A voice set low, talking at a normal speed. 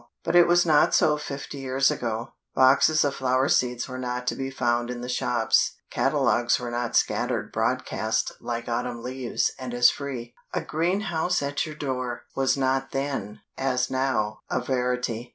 Yes: low, 130 Hz; average, 170 wpm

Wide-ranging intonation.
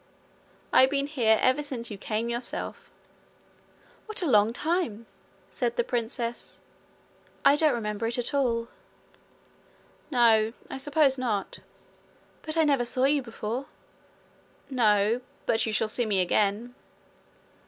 No: average, 4.0 semitones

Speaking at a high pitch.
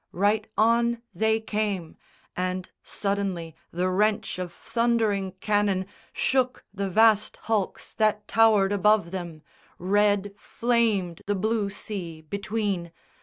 Yes: high, 205 Hz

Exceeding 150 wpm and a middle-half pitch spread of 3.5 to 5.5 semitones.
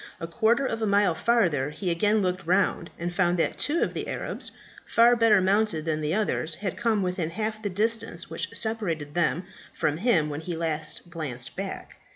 Yes: average, 195 wpm; average, 5.0 semitones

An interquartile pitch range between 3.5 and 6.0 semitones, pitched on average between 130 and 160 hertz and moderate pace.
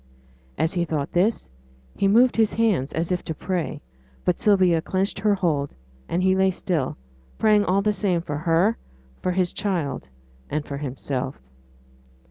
No: average, 4.1 semitones; medium, 180 Hz; average, 160 wpm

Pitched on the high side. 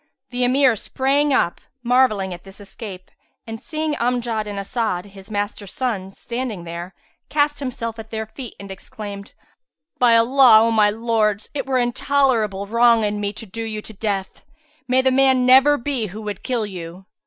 Yes: high, 225 Hz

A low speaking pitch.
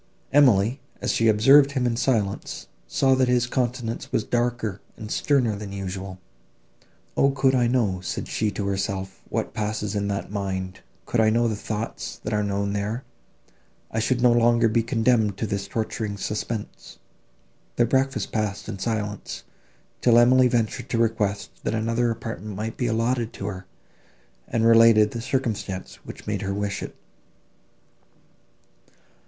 Yes: low, 110 Hz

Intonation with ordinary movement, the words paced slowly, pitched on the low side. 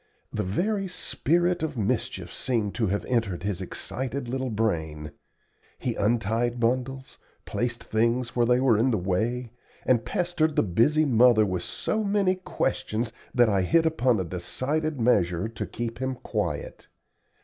No: average, 3.8 semitones; average, 150 wpm; low, 120 Hz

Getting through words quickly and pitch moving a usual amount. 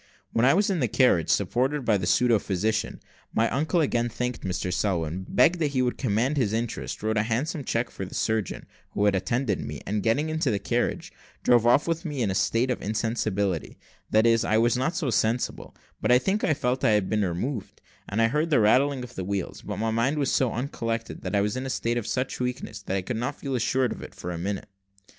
Yes: fast, 240 wpm; average, 4.1 semitones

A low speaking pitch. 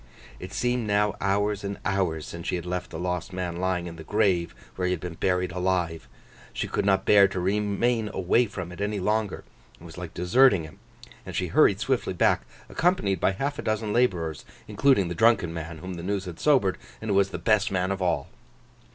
Yes: very low, 95 Hz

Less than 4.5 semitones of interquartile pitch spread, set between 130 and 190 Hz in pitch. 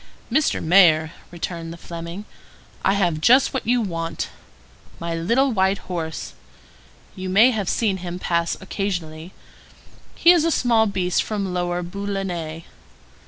Yes: average, 3.4 semitones; medium, 185 Hz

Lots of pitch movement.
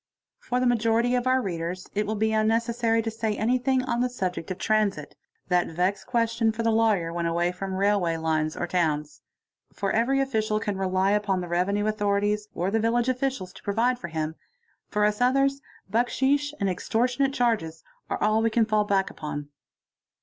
No: average, 4.3 semitones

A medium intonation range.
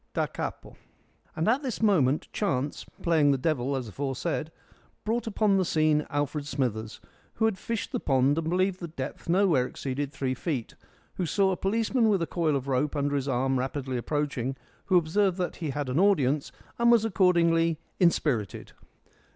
No: wide, 5.7 semitones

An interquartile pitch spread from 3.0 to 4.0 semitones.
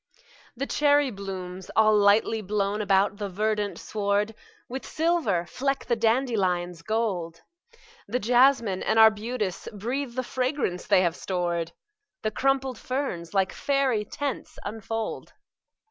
No: average, 4.7 semitones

